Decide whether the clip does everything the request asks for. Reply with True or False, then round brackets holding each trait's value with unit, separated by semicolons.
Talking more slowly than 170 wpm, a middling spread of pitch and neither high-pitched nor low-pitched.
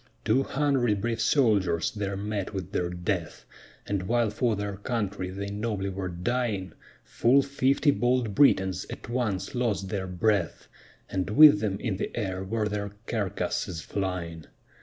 False (150 wpm; 3.9 semitones; 100 Hz)